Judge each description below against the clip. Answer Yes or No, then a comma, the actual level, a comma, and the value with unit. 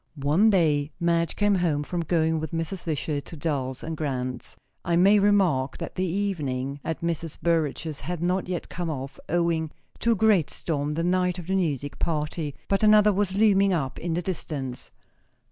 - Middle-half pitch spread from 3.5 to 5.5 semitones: Yes, average, 3.8 semitones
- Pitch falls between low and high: Yes, medium, 165 Hz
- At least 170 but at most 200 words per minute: Yes, average, 180 wpm